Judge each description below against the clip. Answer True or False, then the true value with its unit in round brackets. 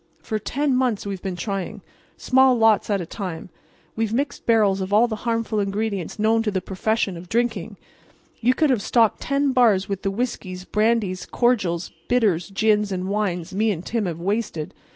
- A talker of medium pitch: False (210 Hz)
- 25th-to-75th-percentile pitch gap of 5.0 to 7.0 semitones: False (3.4 semitones)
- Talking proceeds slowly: False (180 wpm)